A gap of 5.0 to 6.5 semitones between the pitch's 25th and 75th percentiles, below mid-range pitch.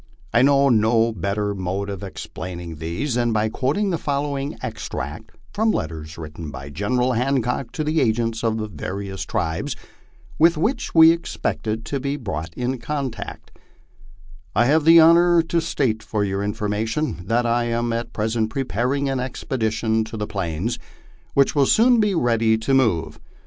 Yes: average, 5.3 semitones; low, 115 Hz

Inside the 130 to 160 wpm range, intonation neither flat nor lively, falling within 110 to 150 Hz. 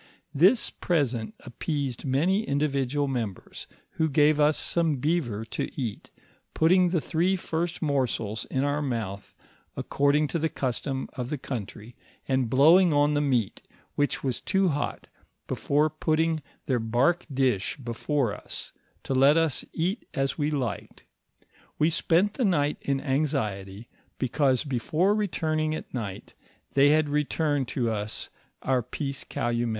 Yes: average, 145 wpm; average, 4.0 semitones; medium, 140 Hz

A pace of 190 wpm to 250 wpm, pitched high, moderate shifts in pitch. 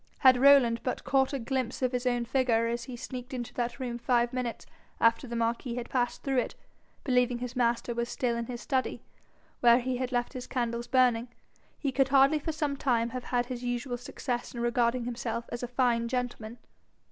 No: fast, 205 wpm; high, 245 Hz; narrow, 1.4 semitones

